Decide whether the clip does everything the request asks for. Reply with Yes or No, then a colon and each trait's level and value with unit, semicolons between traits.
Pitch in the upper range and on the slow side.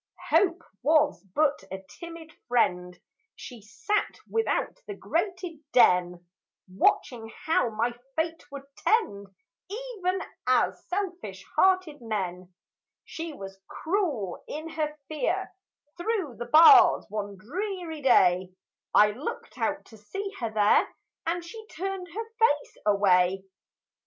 Yes: very high, 300 Hz; slow, 120 wpm